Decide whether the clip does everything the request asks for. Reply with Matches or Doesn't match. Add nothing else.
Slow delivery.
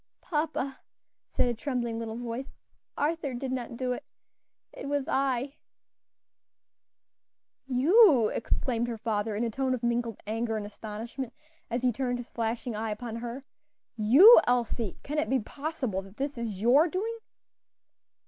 Doesn't match